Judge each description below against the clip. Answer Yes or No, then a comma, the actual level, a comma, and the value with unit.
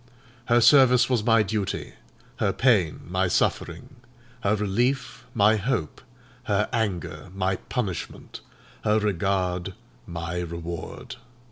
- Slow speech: Yes, slow, 90 wpm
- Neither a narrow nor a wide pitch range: Yes, average, 4.5 semitones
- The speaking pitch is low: Yes, low, 105 Hz